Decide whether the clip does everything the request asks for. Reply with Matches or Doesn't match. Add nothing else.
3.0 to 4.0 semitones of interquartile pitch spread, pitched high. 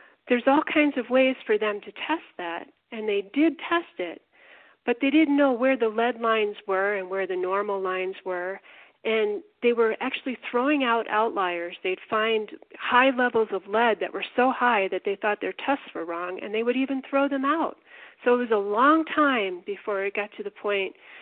Doesn't match